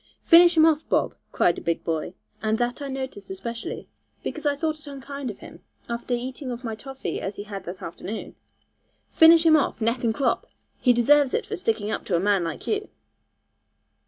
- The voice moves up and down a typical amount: No, wide, 5.8 semitones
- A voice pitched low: No, high, 245 Hz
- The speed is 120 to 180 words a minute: No, average, 200 wpm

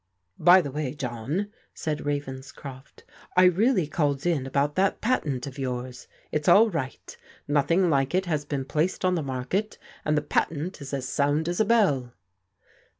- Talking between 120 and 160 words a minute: No, average, 170 wpm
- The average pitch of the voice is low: No, medium, 145 Hz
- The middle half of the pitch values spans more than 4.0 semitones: Yes, average, 4.7 semitones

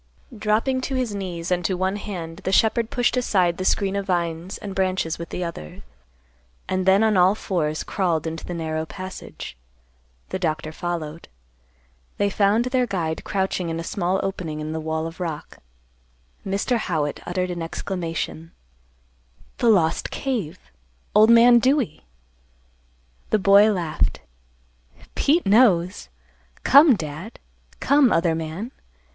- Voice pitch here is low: No, medium, 185 Hz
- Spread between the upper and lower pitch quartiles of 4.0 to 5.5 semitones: Yes, average, 4.4 semitones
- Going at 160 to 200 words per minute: No, average, 140 wpm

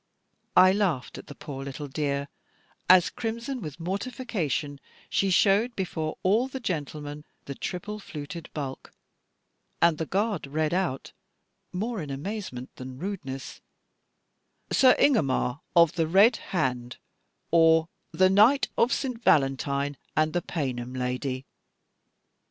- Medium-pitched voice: Yes, medium, 165 Hz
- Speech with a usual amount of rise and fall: No, wide, 6.3 semitones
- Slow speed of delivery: Yes, slow, 125 wpm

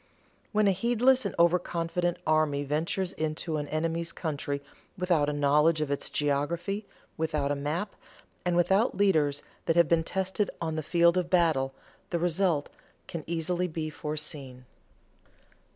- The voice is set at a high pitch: No, medium, 165 Hz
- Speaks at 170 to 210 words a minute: No, average, 150 wpm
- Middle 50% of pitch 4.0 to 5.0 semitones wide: No, average, 3.0 semitones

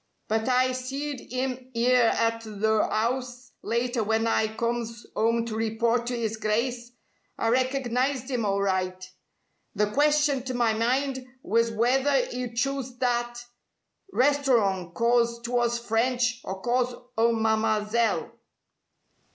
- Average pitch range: No, narrow, 2.2 semitones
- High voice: Yes, high, 235 Hz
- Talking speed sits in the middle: No, slow, 125 wpm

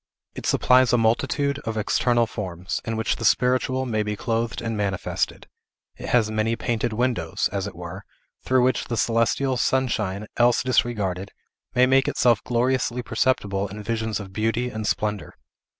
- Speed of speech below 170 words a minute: Yes, average, 160 wpm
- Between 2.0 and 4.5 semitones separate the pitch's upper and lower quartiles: Yes, average, 2.9 semitones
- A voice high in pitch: No, low, 115 Hz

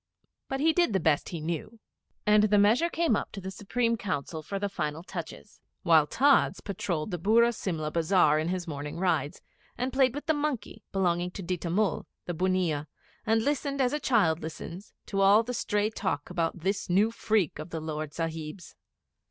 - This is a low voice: No, high, 190 Hz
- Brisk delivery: No, average, 190 wpm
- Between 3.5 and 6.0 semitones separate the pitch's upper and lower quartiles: Yes, wide, 5.4 semitones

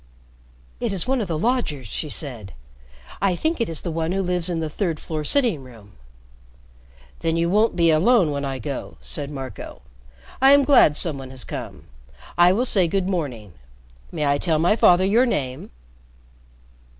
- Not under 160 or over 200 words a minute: Yes, average, 180 wpm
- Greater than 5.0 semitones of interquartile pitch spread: Yes, wide, 5.5 semitones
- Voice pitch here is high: No, medium, 165 Hz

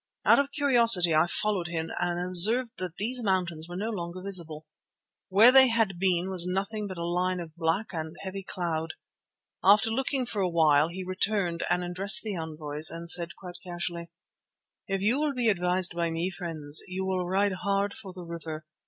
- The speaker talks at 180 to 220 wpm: Yes, average, 185 wpm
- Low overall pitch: No, medium, 180 Hz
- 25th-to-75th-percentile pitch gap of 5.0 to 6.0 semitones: No, average, 2.9 semitones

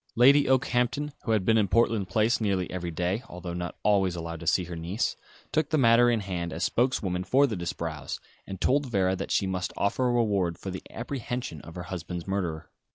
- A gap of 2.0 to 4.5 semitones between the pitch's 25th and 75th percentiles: No, average, 5.3 semitones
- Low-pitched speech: Yes, very low, 95 Hz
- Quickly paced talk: Yes, fast, 210 wpm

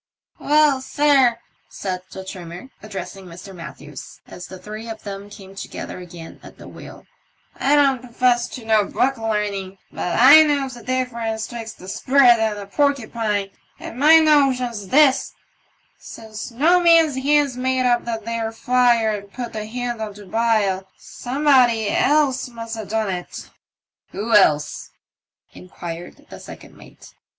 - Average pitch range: Yes, average, 4.4 semitones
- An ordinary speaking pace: Yes, average, 155 wpm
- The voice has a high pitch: Yes, high, 230 Hz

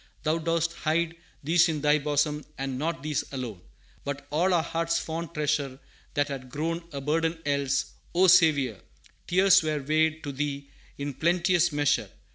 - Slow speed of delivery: No, average, 160 wpm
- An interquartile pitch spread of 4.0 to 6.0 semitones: No, average, 2.8 semitones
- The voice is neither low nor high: Yes, medium, 155 Hz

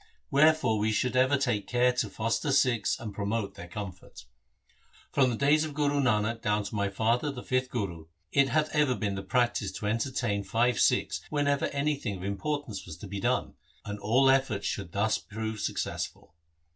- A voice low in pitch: Yes, low, 115 Hz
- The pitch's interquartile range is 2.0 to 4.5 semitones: No, average, 5.0 semitones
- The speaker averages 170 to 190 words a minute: Yes, average, 185 wpm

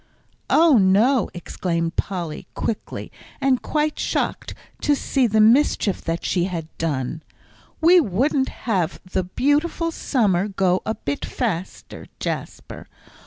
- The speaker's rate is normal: No, slow, 120 wpm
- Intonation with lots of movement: Yes, wide, 7.5 semitones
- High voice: Yes, high, 205 Hz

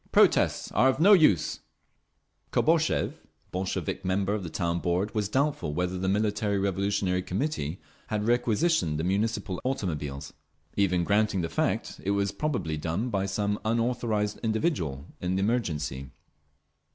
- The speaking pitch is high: No, low, 100 Hz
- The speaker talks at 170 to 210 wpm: No, average, 140 wpm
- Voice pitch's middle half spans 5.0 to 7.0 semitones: No, average, 4.0 semitones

